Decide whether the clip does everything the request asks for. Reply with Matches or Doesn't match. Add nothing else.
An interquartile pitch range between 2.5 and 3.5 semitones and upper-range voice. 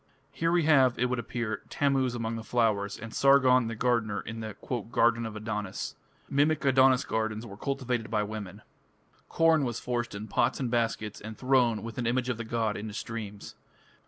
Doesn't match